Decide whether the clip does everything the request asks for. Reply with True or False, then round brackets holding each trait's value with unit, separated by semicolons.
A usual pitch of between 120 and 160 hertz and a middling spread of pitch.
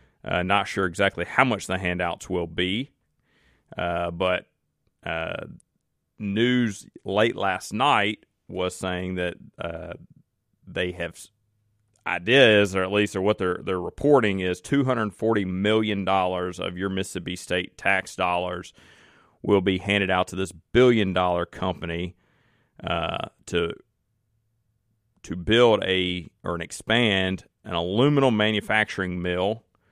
False (95 Hz; 3.1 semitones)